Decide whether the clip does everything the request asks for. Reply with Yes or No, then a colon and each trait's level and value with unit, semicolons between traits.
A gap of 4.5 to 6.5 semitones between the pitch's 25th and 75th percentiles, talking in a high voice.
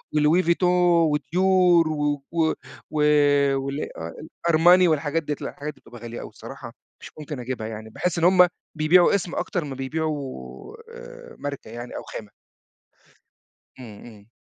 No: average, 5.0 semitones; medium, 150 Hz